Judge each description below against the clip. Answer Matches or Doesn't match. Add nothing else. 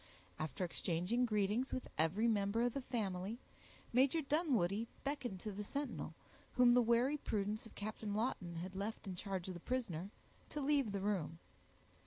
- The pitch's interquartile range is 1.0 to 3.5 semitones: Doesn't match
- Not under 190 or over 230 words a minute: Doesn't match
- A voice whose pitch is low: Doesn't match